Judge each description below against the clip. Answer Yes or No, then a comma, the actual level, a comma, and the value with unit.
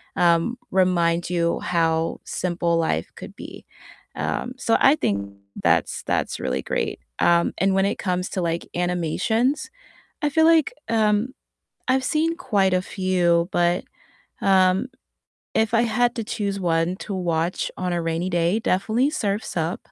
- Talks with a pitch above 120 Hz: Yes, medium, 185 Hz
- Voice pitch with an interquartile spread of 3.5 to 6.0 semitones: Yes, average, 4.5 semitones